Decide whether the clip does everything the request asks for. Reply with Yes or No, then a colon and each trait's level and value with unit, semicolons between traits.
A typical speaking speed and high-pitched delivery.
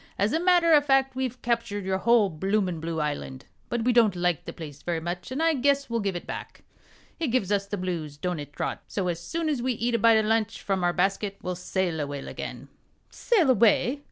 No: fast, 230 wpm; high, 205 Hz